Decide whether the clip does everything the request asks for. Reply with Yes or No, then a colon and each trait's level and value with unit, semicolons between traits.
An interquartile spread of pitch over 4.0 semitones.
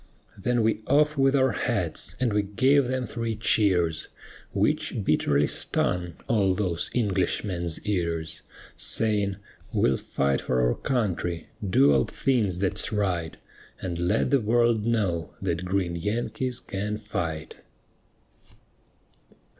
Yes: average, 5.1 semitones